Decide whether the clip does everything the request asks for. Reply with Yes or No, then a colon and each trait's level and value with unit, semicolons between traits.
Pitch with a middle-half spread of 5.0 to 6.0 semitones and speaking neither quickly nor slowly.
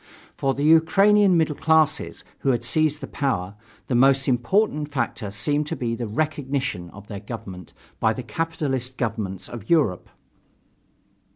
Yes: wide, 5.6 semitones; average, 150 wpm